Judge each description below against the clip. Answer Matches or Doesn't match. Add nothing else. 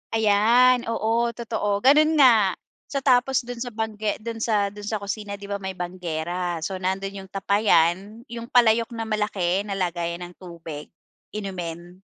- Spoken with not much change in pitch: Doesn't match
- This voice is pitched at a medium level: Doesn't match